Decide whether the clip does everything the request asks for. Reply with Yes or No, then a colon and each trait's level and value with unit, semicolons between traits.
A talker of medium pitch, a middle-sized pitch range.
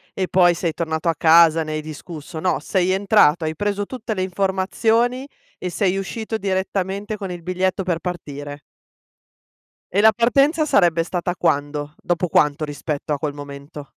Yes: medium, 180 Hz; average, 4.1 semitones